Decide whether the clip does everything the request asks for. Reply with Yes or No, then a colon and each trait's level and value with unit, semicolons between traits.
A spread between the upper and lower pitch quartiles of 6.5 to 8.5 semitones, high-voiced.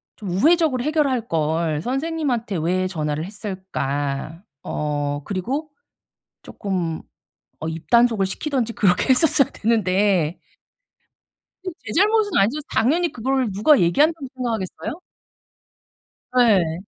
Yes: wide, 8.0 semitones; high, 210 Hz